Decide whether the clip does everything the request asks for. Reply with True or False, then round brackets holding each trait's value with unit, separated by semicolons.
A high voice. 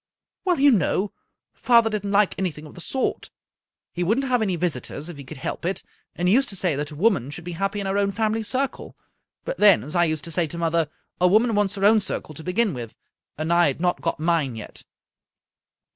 False (180 Hz)